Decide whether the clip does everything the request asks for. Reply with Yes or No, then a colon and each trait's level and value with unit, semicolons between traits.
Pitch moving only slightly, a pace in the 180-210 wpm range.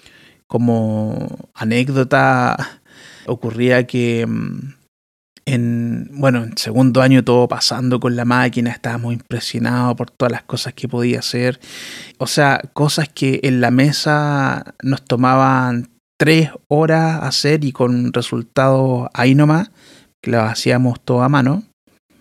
No: narrow, 2.1 semitones; slow, 125 wpm